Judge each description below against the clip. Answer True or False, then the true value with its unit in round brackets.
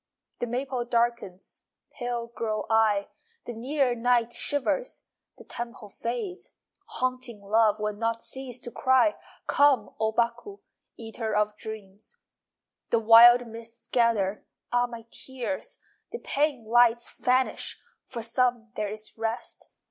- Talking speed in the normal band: False (125 wpm)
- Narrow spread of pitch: True (2.1 semitones)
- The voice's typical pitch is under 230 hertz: False (235 Hz)